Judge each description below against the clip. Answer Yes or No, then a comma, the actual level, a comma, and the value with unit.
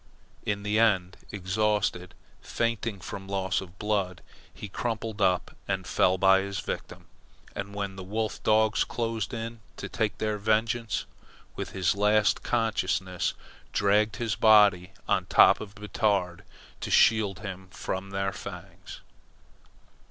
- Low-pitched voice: Yes, low, 100 Hz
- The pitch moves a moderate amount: No, narrow, 2.3 semitones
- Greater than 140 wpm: No, slow, 135 wpm